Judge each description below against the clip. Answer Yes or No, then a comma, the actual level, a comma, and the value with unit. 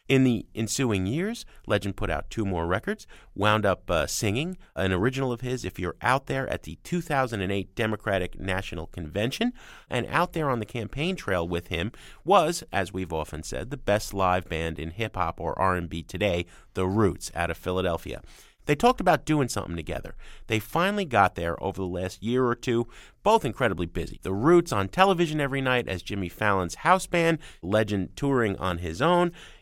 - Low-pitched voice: Yes, low, 100 Hz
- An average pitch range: No, wide, 6.5 semitones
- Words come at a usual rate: Yes, average, 185 wpm